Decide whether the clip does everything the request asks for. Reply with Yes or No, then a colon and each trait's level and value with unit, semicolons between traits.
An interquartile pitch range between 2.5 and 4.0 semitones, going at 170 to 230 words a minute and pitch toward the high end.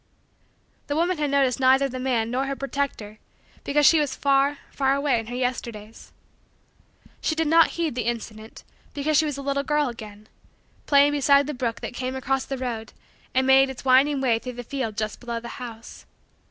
Yes: average, 2.9 semitones; average, 195 wpm; very high, 265 Hz